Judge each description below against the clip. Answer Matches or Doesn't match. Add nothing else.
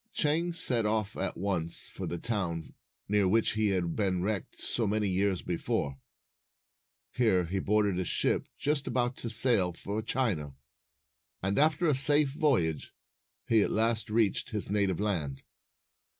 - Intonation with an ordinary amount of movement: Matches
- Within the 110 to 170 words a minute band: Matches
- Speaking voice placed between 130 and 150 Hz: Doesn't match